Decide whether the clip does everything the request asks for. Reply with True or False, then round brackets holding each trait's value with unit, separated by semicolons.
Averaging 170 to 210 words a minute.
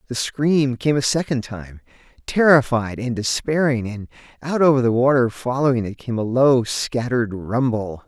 False (155 wpm)